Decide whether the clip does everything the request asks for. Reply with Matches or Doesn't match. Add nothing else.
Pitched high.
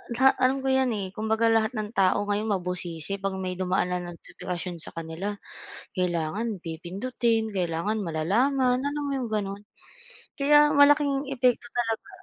Matches